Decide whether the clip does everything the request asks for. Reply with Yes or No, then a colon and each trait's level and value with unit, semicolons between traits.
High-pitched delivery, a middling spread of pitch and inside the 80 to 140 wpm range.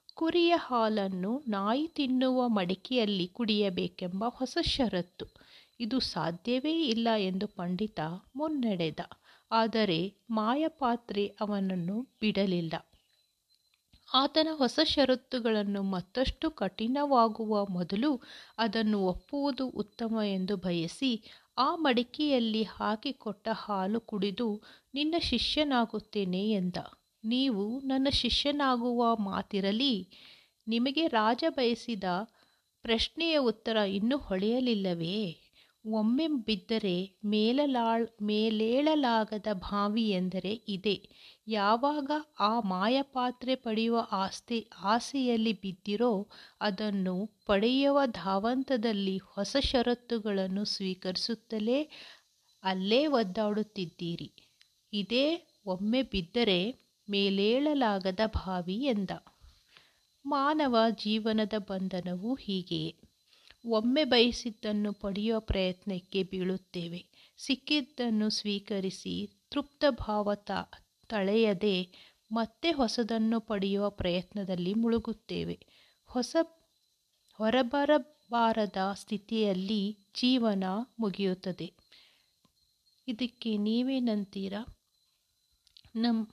No: high, 220 Hz; average, 4.0 semitones; average, 70 wpm